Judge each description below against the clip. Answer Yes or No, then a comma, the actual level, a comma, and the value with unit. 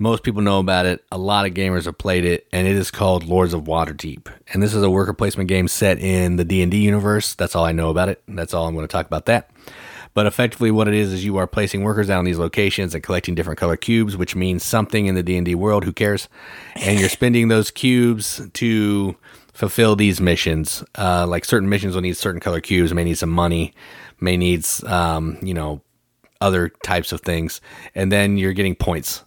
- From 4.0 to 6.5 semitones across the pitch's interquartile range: No, average, 3.0 semitones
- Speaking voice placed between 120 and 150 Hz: No, very low, 95 Hz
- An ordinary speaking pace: No, fast, 230 wpm